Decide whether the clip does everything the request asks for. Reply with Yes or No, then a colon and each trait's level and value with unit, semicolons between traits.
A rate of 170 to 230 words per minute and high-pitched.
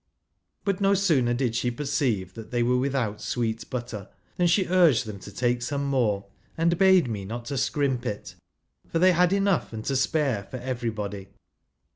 No: average, 185 wpm; low, 125 Hz